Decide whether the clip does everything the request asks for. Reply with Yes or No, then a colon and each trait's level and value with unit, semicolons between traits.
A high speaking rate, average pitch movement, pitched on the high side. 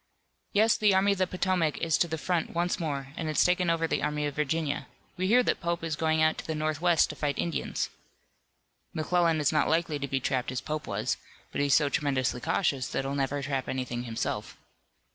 No: fast, 215 wpm; average, 3.4 semitones; medium, 155 Hz